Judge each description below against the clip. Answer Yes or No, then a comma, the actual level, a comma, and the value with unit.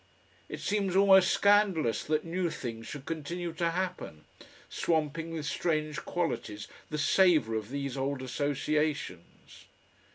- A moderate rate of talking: No, slow, 125 wpm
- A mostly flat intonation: No, average, 4.1 semitones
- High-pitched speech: No, medium, 155 Hz